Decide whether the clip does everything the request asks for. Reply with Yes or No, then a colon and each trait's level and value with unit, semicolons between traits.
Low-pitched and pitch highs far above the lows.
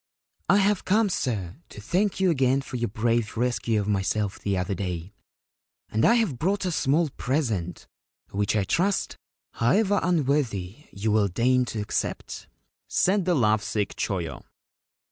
Yes: low, 120 Hz; wide, 8.8 semitones